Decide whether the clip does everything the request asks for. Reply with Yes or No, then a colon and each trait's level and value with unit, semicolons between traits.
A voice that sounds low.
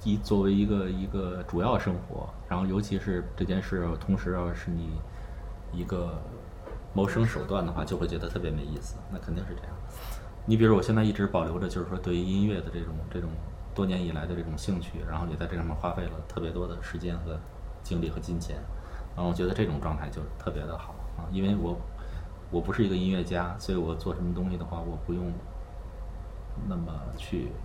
Yes: very low, 90 Hz